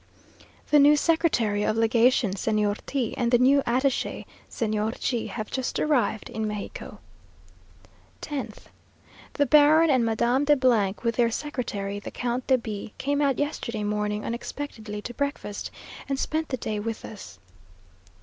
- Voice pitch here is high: Yes, high, 235 Hz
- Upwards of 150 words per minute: No, average, 145 wpm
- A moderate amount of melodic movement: Yes, average, 4.7 semitones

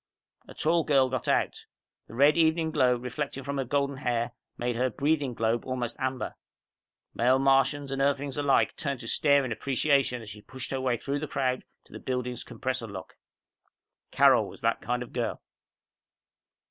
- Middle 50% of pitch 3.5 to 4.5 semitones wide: No, narrow, 2.4 semitones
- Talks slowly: No, average, 175 wpm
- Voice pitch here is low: Yes, low, 130 Hz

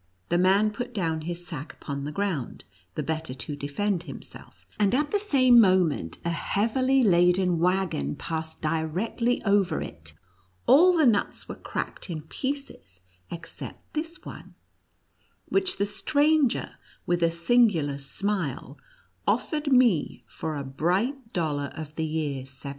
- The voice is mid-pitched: Yes, medium, 175 Hz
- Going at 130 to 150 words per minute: Yes, average, 140 wpm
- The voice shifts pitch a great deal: Yes, wide, 7.2 semitones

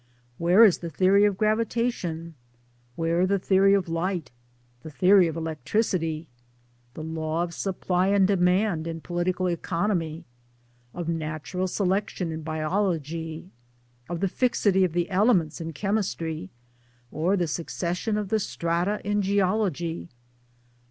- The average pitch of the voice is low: No, medium, 180 Hz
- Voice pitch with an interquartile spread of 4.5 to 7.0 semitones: No, average, 3.2 semitones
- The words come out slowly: Yes, slow, 130 wpm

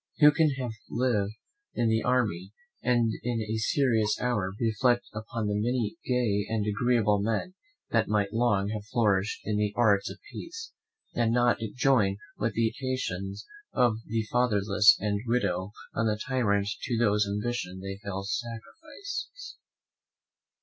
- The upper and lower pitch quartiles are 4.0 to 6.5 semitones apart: No, average, 3.1 semitones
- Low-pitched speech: Yes, low, 110 Hz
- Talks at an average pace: Yes, average, 145 wpm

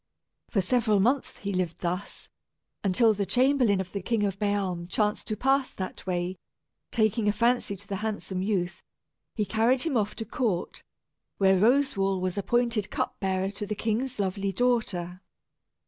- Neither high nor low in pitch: No, high, 205 Hz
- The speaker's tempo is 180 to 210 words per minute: No, average, 165 wpm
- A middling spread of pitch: Yes, average, 3.5 semitones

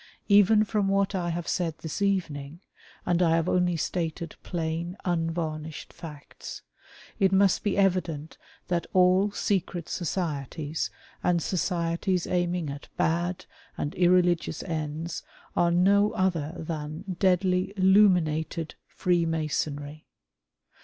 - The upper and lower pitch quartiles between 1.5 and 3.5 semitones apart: Yes, narrow, 2.6 semitones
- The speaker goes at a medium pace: No, slow, 120 wpm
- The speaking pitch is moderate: Yes, medium, 175 Hz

